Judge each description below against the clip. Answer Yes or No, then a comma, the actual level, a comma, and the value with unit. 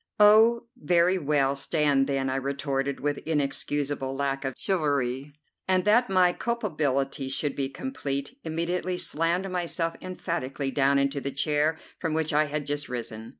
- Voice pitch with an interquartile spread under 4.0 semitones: No, average, 4.3 semitones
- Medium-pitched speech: Yes, medium, 145 Hz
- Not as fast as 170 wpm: Yes, average, 150 wpm